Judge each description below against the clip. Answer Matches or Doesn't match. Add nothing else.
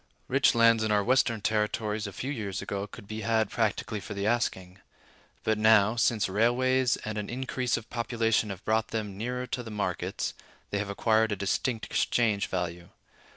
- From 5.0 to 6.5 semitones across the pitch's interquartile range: Doesn't match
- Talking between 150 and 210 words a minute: Matches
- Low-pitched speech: Matches